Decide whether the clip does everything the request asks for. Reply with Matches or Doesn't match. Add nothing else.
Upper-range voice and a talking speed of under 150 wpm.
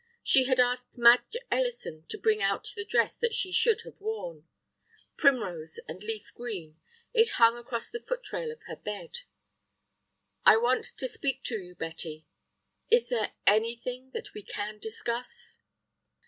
Doesn't match